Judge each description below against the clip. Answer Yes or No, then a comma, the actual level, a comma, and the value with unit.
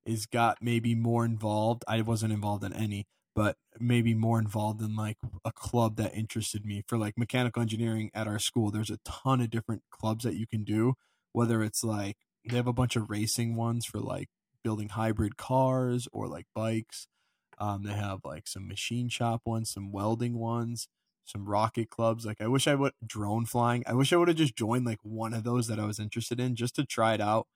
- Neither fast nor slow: No, fast, 215 wpm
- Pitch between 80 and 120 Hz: Yes, low, 115 Hz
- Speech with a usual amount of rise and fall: No, narrow, 1.8 semitones